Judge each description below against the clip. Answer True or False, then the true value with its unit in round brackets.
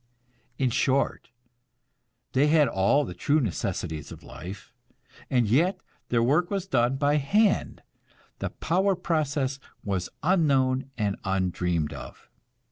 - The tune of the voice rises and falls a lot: True (7.5 semitones)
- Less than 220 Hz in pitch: True (135 Hz)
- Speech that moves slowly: True (125 wpm)